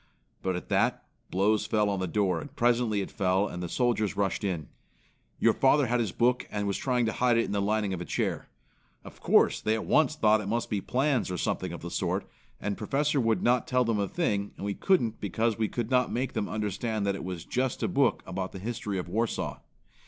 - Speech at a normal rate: No, fast, 235 wpm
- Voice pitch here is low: Yes, low, 110 Hz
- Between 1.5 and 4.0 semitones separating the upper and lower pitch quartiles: Yes, average, 3.5 semitones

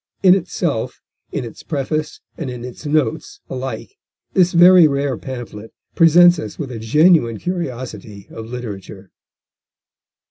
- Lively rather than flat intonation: Yes, wide, 6.5 semitones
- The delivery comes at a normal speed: No, slow, 130 wpm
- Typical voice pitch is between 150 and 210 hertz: No, low, 135 Hz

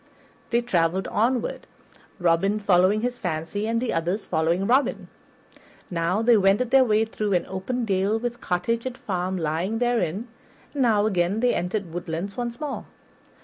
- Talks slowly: No, average, 155 wpm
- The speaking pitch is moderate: No, high, 205 Hz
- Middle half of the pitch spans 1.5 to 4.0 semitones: No, average, 4.9 semitones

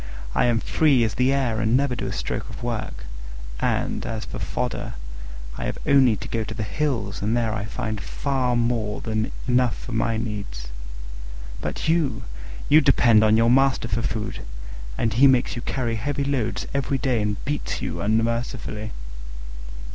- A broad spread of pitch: No, average, 3.0 semitones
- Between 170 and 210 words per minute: Yes, average, 175 wpm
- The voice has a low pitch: Yes, low, 115 Hz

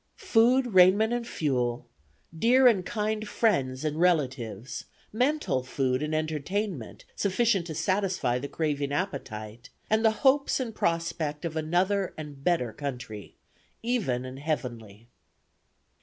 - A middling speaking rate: No, slow, 125 wpm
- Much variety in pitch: Yes, wide, 8.3 semitones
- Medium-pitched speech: Yes, medium, 160 Hz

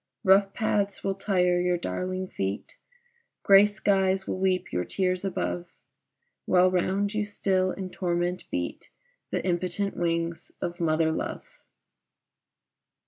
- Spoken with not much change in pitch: Yes, narrow, 2.1 semitones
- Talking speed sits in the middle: No, slow, 125 wpm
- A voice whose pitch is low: No, medium, 185 Hz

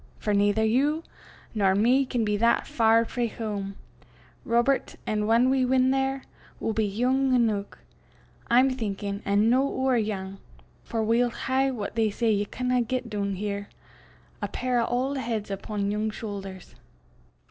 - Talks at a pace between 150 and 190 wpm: Yes, average, 160 wpm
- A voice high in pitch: Yes, high, 225 Hz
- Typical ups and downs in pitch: Yes, average, 3.6 semitones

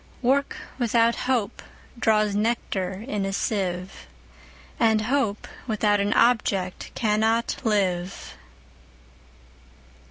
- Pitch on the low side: No, high, 215 Hz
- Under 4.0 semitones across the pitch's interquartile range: Yes, average, 2.9 semitones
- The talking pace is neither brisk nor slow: No, slow, 90 wpm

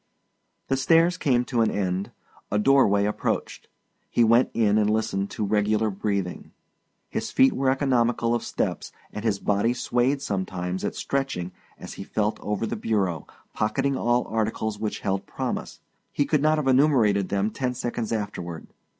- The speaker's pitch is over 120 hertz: No, low, 110 Hz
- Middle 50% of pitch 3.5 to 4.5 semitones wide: Yes, average, 4.1 semitones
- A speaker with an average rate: Yes, average, 160 wpm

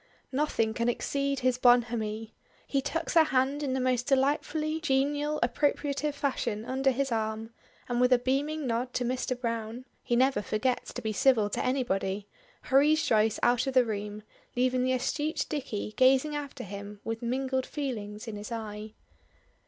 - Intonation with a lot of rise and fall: No, average, 3.7 semitones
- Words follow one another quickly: No, average, 165 wpm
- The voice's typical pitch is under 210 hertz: No, very high, 255 Hz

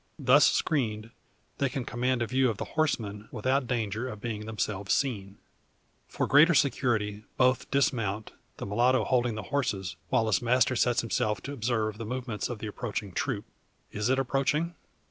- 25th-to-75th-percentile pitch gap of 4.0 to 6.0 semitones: No, average, 3.6 semitones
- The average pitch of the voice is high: No, low, 120 Hz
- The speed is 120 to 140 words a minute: No, average, 165 wpm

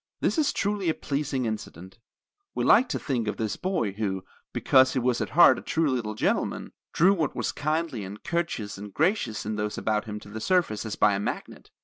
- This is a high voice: No, low, 120 Hz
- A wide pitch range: Yes, wide, 7.4 semitones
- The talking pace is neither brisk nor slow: No, fast, 215 wpm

